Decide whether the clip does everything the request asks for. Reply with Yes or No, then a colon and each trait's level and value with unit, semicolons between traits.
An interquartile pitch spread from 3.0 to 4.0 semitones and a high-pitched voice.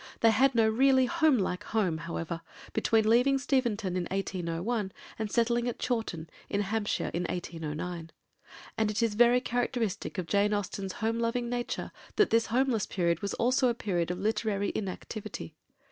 No: average, 4.5 semitones; high, 220 Hz